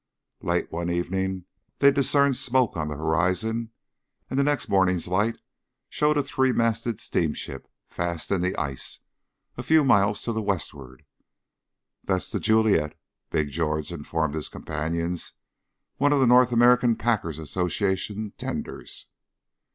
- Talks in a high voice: No, very low, 95 Hz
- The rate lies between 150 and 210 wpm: No, slow, 135 wpm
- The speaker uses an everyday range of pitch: No, wide, 6.4 semitones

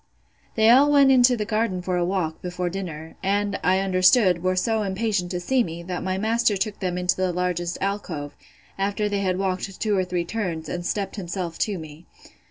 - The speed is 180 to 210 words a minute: Yes, average, 200 wpm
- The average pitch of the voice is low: No, medium, 185 Hz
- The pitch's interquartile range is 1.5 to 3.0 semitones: Yes, average, 2.7 semitones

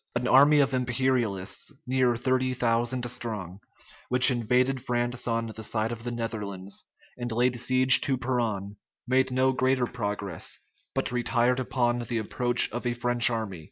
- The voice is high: No, low, 120 Hz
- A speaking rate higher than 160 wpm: No, average, 155 wpm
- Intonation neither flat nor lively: No, narrow, 2.0 semitones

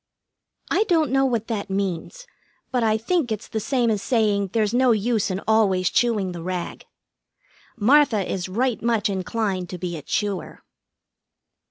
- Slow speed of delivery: No, average, 160 wpm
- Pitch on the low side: No, high, 215 Hz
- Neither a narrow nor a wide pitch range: Yes, average, 4.0 semitones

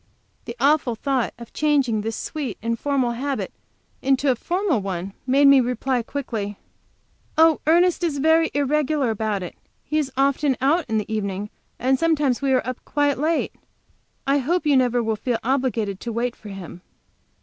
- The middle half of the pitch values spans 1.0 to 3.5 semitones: No, average, 4.4 semitones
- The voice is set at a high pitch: Yes, very high, 265 Hz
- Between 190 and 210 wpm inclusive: No, average, 165 wpm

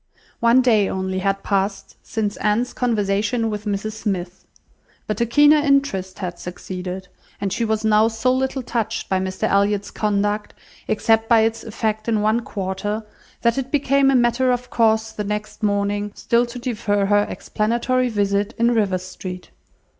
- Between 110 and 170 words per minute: Yes, average, 160 wpm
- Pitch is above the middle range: Yes, high, 215 Hz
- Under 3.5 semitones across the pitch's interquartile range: Yes, average, 2.9 semitones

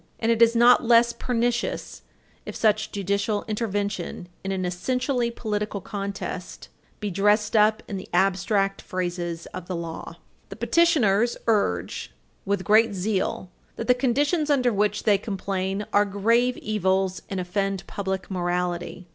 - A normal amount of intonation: Yes, average, 3.3 semitones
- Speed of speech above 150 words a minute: No, average, 140 wpm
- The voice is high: Yes, high, 205 Hz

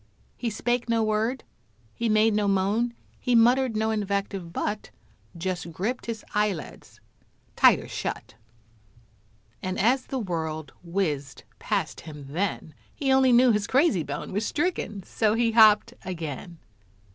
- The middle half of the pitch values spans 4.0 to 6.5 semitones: Yes, average, 4.3 semitones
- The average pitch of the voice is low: No, high, 210 Hz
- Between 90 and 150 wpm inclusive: Yes, slow, 135 wpm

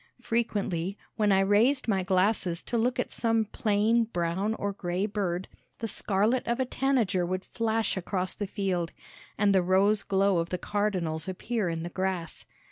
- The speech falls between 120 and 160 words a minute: No, average, 170 wpm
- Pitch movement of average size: Yes, average, 3.2 semitones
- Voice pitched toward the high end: Yes, high, 200 Hz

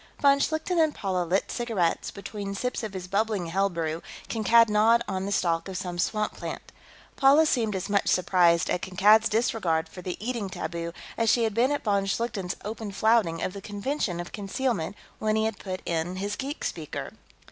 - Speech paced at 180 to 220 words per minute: Yes, average, 190 wpm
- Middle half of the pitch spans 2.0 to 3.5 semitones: No, average, 3.9 semitones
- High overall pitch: Yes, high, 200 Hz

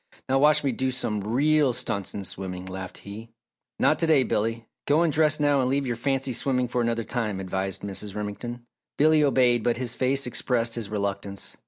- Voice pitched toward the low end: Yes, low, 120 Hz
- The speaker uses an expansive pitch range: No, average, 4.6 semitones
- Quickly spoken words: No, average, 195 wpm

